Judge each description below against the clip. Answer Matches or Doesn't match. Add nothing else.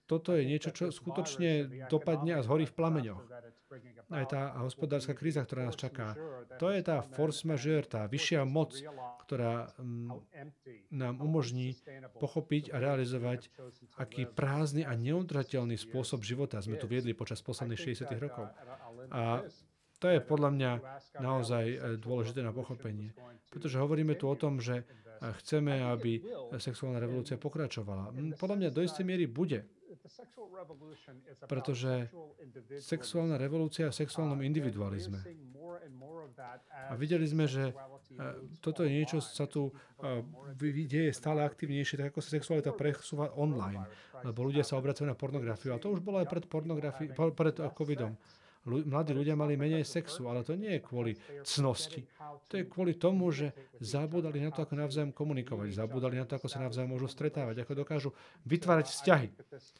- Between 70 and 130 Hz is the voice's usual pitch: Doesn't match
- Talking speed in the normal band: Matches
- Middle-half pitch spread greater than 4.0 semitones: Doesn't match